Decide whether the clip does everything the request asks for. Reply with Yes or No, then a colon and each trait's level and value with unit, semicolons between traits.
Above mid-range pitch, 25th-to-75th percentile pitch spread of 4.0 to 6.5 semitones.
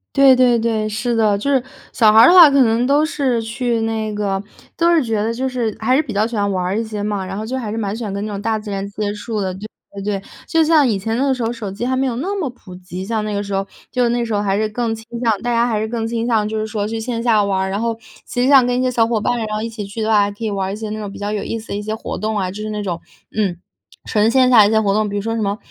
No: high, 220 Hz; average, 2.7 semitones